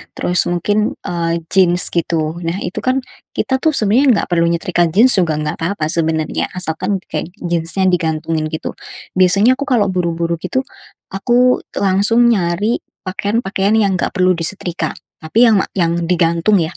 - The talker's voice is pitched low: No, medium, 180 Hz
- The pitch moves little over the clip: No, average, 3.7 semitones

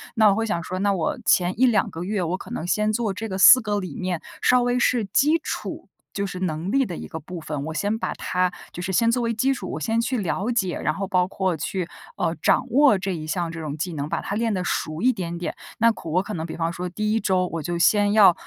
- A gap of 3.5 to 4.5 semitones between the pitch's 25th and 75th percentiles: Yes, average, 4.2 semitones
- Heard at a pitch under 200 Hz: Yes, high, 190 Hz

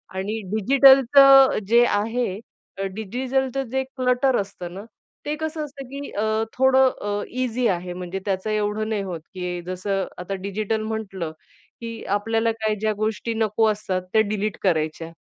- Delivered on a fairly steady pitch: No, average, 4.5 semitones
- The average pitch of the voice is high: Yes, high, 215 Hz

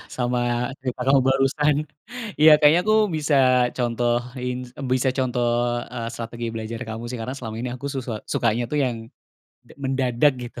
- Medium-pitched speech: No, low, 125 Hz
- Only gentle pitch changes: Yes, narrow, 2.2 semitones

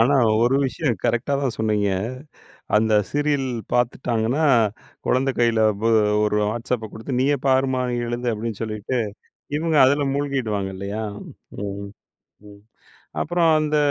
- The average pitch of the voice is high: No, low, 120 Hz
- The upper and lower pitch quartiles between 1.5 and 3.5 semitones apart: No, average, 4.0 semitones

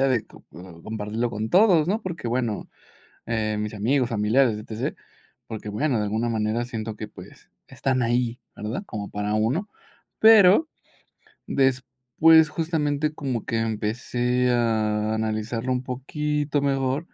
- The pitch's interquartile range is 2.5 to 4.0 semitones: No, average, 4.6 semitones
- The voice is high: No, low, 120 Hz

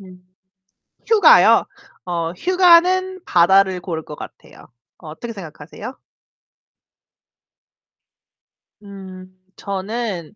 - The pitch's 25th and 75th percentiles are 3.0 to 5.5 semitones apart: Yes, average, 5.1 semitones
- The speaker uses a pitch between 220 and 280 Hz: No, high, 190 Hz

